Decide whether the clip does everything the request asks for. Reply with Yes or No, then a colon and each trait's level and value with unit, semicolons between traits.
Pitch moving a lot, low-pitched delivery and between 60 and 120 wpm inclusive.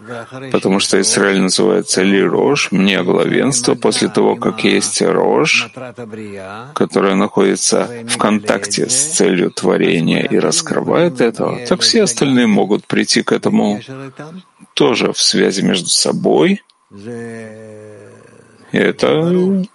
Yes: wide, 7.3 semitones; low, 120 Hz; slow, 110 wpm